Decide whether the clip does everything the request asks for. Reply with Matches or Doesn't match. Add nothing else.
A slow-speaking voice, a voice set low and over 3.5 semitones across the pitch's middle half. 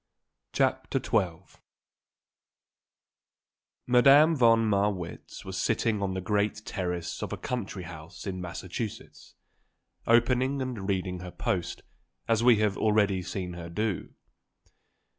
Matches